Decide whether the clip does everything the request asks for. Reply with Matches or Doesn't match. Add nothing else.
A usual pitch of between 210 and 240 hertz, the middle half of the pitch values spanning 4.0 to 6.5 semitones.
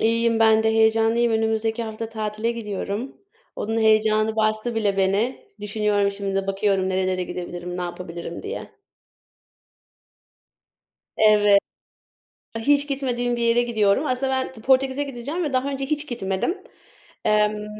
Doesn't match